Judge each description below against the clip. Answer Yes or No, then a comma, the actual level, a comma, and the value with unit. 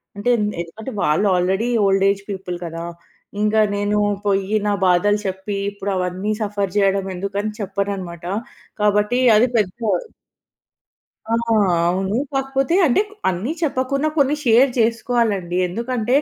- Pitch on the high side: Yes, high, 205 Hz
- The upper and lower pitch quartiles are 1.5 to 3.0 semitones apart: No, average, 3.4 semitones